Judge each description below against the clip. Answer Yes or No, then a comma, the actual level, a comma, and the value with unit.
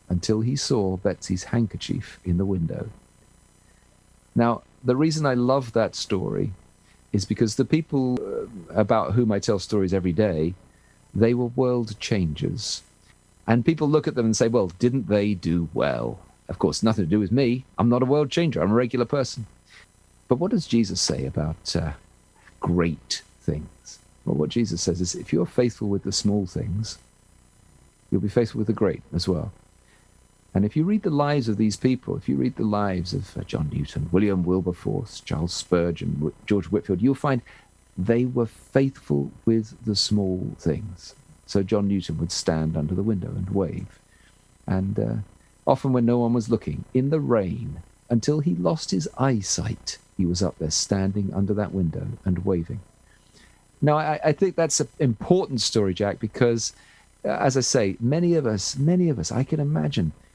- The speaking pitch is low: Yes, low, 105 Hz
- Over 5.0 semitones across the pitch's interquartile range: Yes, wide, 5.5 semitones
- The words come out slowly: No, average, 175 wpm